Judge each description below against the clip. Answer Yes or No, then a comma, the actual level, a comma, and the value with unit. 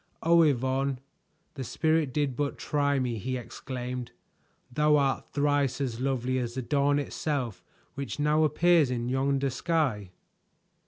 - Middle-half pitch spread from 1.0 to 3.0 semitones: Yes, narrow, 2.6 semitones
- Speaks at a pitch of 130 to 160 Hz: Yes, low, 135 Hz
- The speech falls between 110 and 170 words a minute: Yes, average, 140 wpm